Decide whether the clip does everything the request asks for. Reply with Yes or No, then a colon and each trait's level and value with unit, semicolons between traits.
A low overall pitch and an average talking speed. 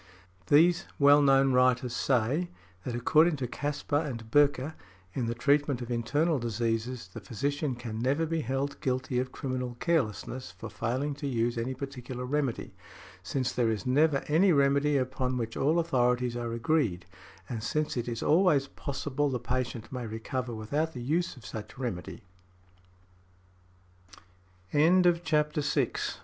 Yes: low, 130 Hz; average, 150 wpm